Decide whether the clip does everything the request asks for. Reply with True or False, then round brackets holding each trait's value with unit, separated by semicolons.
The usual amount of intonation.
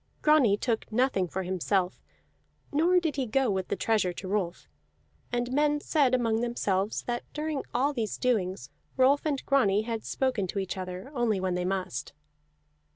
False (6.0 semitones)